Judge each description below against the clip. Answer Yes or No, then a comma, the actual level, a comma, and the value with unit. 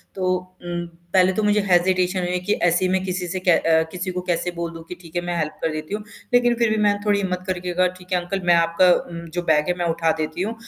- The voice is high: No, medium, 180 Hz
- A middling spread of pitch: No, narrow, 1.6 semitones